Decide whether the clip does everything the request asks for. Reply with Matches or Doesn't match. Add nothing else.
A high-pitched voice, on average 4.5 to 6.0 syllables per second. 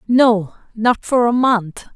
Doesn't match